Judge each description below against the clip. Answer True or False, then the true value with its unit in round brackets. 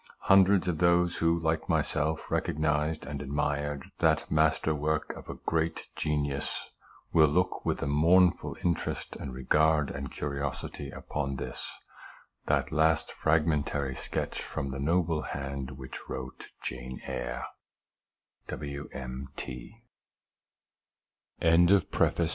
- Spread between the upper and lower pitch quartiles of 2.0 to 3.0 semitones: True (2.6 semitones)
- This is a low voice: True (75 Hz)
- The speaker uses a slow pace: True (105 wpm)